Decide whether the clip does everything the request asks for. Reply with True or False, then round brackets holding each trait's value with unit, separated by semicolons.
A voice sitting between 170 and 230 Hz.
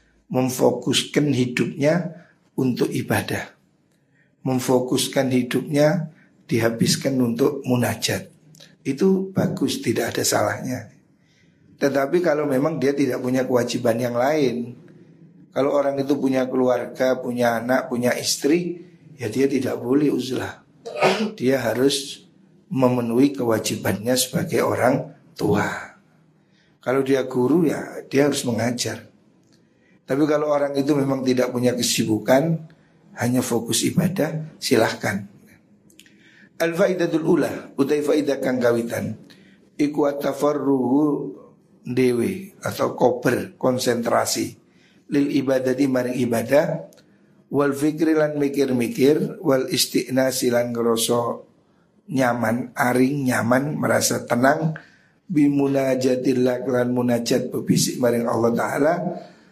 False (135 Hz)